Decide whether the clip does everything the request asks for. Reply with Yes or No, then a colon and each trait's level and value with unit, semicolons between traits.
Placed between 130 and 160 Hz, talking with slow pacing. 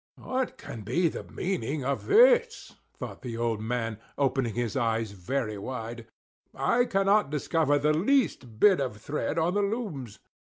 No: medium, 140 Hz; average, 155 wpm